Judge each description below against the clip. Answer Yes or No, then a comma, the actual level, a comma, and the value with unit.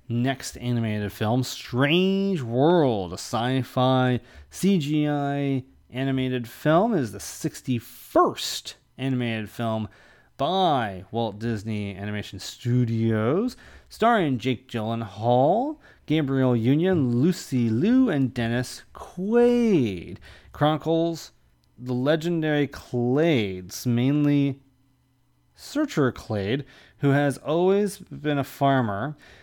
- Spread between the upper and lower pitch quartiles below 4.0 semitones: No, average, 4.6 semitones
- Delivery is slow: Yes, slow, 90 wpm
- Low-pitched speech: Yes, low, 130 Hz